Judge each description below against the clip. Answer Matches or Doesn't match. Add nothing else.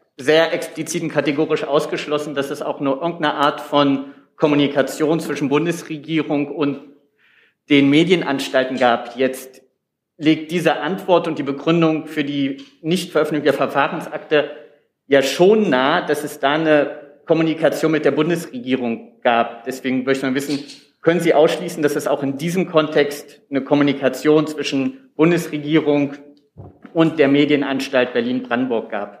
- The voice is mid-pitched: Matches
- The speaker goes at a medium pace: Matches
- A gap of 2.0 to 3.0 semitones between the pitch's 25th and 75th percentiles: Matches